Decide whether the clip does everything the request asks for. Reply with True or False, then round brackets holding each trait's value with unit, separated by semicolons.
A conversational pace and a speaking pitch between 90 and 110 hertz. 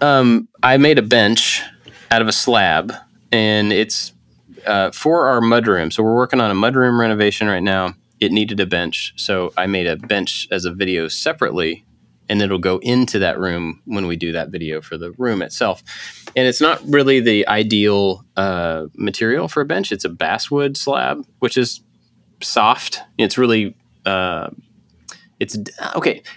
True (175 wpm; 105 Hz)